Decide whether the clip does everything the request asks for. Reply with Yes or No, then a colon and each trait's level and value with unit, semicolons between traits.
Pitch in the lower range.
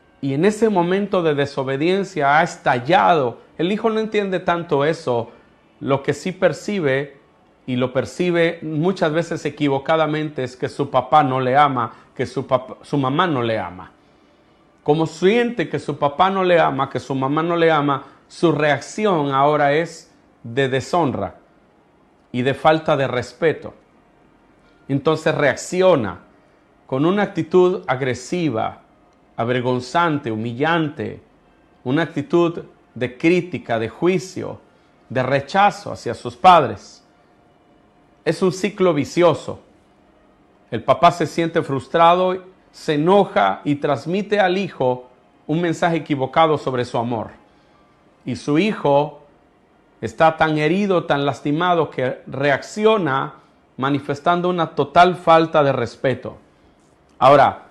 No: medium, 150 Hz